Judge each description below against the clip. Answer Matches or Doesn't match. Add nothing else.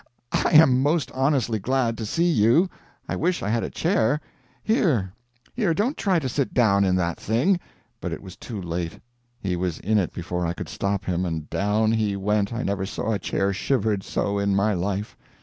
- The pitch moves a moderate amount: Doesn't match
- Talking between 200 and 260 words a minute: Matches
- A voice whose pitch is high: Doesn't match